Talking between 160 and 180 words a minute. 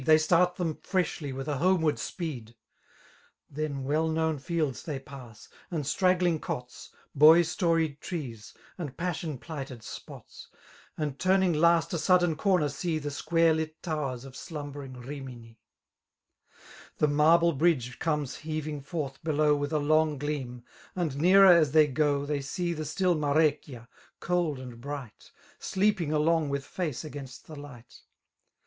No: average, 145 wpm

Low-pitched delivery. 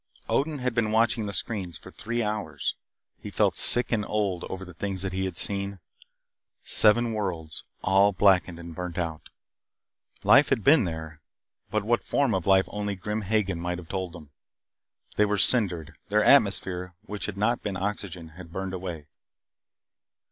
Yes: very low, 95 Hz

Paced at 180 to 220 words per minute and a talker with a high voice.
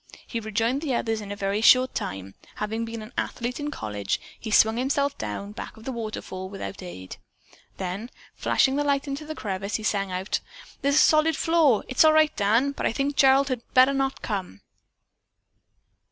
Yes: average, 190 wpm; high, 230 Hz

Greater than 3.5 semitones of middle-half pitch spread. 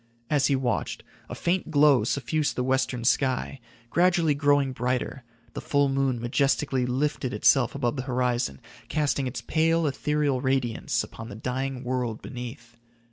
No: narrow, 2.5 semitones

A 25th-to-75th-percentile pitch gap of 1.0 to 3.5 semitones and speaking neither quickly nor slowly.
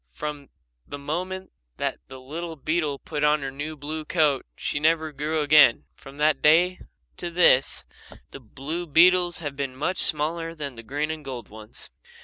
Yes: average, 2.9 semitones; average, 170 wpm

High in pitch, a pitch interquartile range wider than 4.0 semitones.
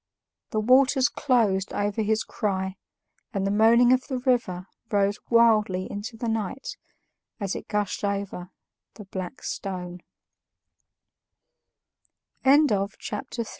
No: high, 210 Hz; average, 3.2 semitones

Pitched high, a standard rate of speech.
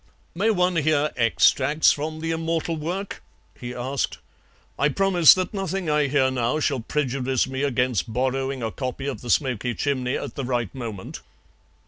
No: medium, 140 Hz; average, 165 wpm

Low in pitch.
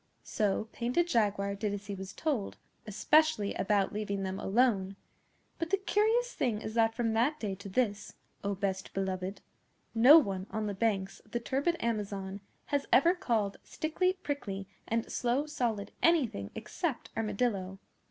No: high, 215 Hz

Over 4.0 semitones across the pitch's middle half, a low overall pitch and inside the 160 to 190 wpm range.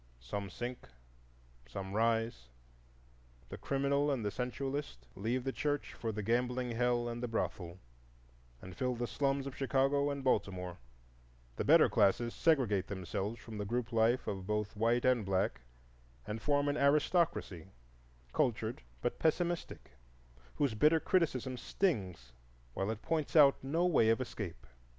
No: average, 5.0 semitones; low, 120 Hz; average, 145 wpm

